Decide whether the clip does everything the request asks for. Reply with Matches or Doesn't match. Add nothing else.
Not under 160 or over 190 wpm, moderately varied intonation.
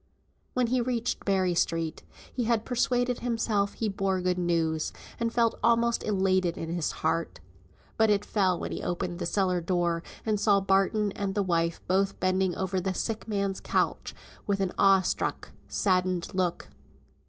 Matches